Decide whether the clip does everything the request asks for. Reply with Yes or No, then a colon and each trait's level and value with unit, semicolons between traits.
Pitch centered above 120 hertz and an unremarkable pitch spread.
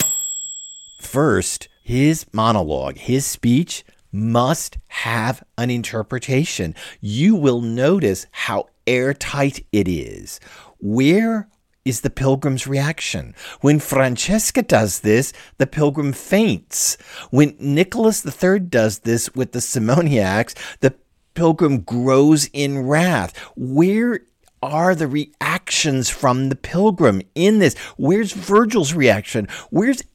No: low, 135 Hz; wide, 5.8 semitones